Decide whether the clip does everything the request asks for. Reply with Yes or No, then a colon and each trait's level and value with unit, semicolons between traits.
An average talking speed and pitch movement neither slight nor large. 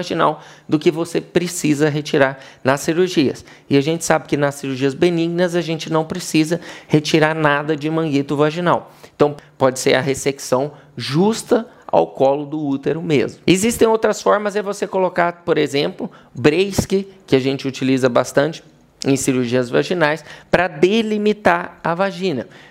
Yes: average, 150 wpm; average, 4.3 semitones